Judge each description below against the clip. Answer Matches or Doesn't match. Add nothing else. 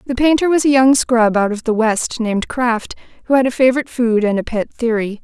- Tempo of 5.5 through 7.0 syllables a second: Matches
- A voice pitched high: Matches